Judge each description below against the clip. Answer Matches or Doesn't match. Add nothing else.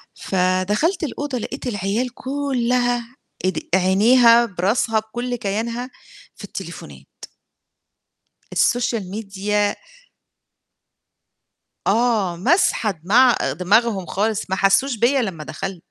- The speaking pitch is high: Matches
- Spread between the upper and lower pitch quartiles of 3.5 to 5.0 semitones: Matches